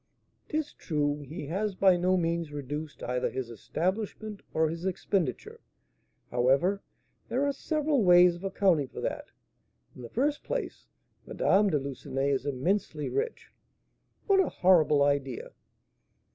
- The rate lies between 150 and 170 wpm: No, slow, 135 wpm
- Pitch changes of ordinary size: No, wide, 6.1 semitones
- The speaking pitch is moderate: Yes, medium, 170 Hz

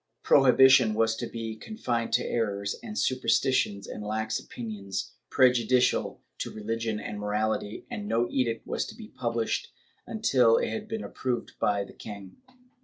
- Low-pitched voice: Yes, low, 115 Hz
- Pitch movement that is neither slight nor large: Yes, average, 3.3 semitones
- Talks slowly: No, average, 155 wpm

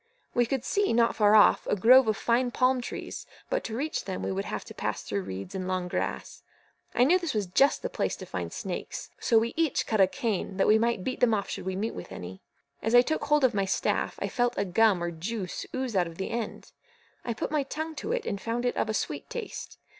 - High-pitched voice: Yes, high, 225 Hz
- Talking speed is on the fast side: Yes, fast, 250 wpm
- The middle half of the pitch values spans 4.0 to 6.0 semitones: Yes, average, 5.2 semitones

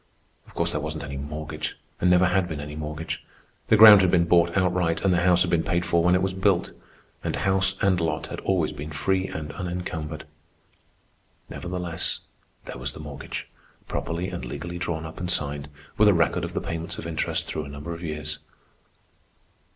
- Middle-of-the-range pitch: No, very low, 85 Hz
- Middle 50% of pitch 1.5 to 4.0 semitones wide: Yes, average, 2.9 semitones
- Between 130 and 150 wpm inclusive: No, average, 195 wpm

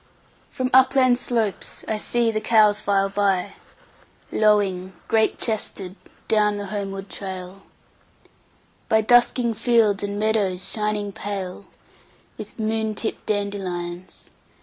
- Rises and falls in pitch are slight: Yes, narrow, 2.1 semitones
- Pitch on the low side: No, high, 205 Hz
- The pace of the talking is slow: Yes, slow, 100 wpm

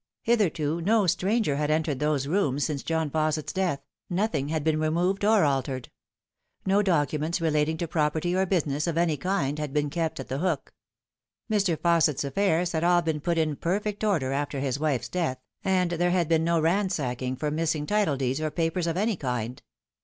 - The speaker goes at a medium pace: Yes, average, 185 wpm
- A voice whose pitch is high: No, medium, 160 Hz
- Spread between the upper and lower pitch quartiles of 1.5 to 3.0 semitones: No, average, 3.5 semitones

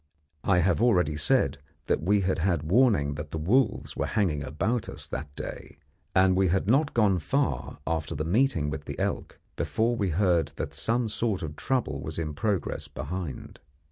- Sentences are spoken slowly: No, average, 180 wpm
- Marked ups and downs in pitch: Yes, wide, 6.1 semitones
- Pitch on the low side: Yes, very low, 90 Hz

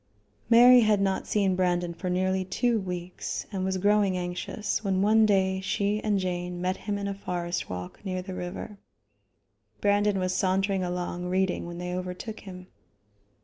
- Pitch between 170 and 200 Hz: Yes, high, 190 Hz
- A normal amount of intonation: No, narrow, 2.1 semitones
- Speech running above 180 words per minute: No, average, 165 wpm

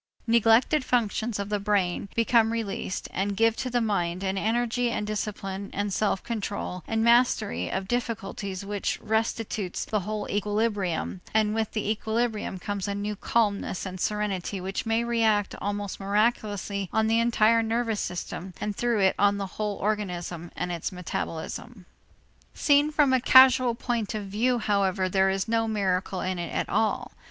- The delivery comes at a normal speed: Yes, average, 165 wpm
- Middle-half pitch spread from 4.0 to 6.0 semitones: No, average, 2.8 semitones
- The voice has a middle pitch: No, high, 210 Hz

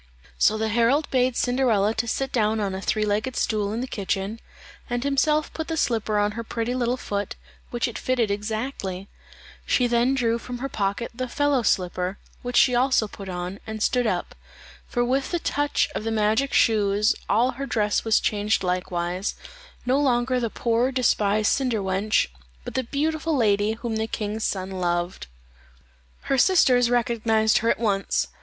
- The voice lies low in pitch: No, high, 230 Hz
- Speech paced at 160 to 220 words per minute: Yes, average, 175 wpm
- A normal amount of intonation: Yes, average, 3.5 semitones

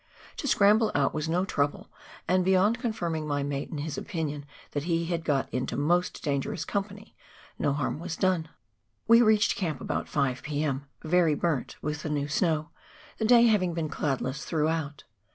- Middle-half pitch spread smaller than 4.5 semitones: Yes, average, 4.1 semitones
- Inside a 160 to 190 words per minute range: Yes, average, 170 wpm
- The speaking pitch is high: No, medium, 160 Hz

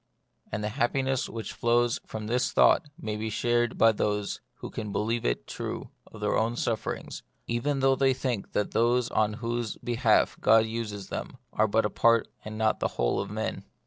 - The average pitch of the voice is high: No, low, 115 Hz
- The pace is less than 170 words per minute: No, average, 190 wpm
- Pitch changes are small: Yes, narrow, 2.0 semitones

